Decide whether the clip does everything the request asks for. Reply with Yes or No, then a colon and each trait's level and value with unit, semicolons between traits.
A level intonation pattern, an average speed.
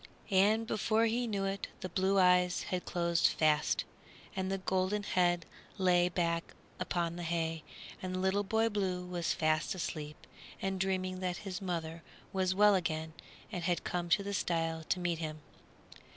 Yes: narrow, 2.3 semitones; average, 165 wpm